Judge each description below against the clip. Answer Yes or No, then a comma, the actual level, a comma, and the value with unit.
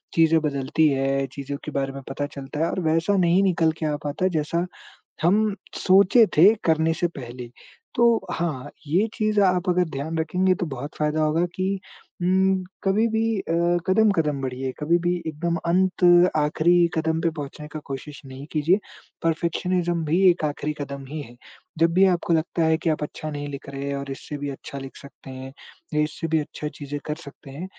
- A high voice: No, medium, 160 Hz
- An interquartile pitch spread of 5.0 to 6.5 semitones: No, average, 3.8 semitones